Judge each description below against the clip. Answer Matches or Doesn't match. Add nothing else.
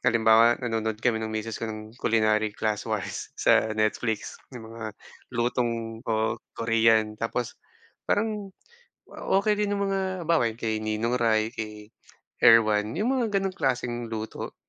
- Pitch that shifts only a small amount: Matches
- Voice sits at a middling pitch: Doesn't match